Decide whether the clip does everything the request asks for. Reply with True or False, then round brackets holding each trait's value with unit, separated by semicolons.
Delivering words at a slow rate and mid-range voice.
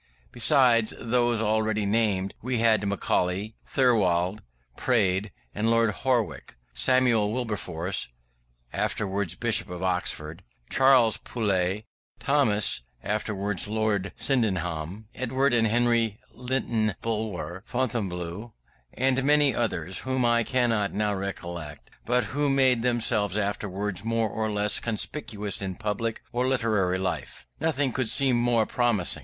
False (115 wpm; 110 Hz)